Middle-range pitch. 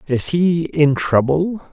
Yes: medium, 160 Hz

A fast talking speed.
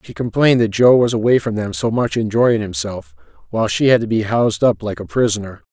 Yes: fast, 230 wpm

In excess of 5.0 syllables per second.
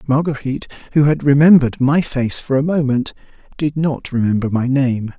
Yes: 5.3 syllables/s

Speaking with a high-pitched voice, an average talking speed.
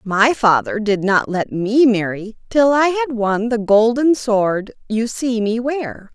Yes: high, 225 Hz; average, 175 wpm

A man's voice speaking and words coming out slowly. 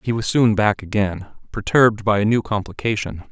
No: male; average, 200 wpm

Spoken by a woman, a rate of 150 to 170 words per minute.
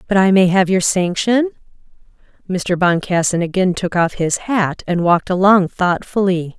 Yes: female; average, 155 wpm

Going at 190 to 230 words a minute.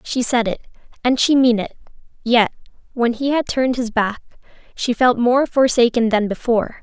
No: average, 175 wpm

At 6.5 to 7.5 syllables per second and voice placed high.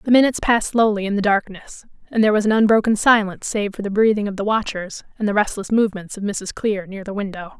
Yes: 6.6 syllables/s; high, 205 Hz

